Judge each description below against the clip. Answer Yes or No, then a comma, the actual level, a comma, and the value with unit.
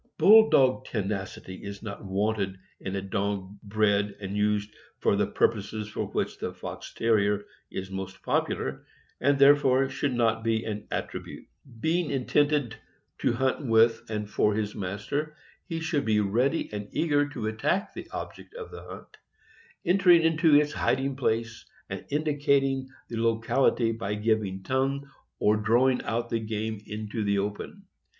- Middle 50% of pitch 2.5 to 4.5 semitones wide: No, average, 5.0 semitones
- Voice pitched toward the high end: No, low, 115 Hz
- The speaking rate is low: No, average, 155 wpm